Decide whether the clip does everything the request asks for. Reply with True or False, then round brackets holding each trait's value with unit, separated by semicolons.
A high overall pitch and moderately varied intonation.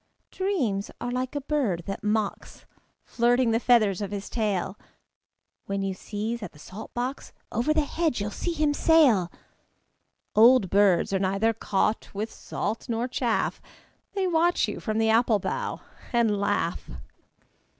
True (225 Hz; 4.3 semitones)